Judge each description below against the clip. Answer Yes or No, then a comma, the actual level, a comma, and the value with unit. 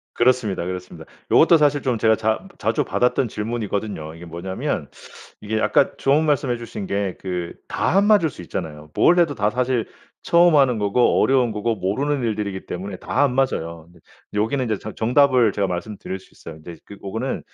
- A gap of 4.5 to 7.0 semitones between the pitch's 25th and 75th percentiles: Yes, wide, 5.5 semitones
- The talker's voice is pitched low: Yes, low, 110 Hz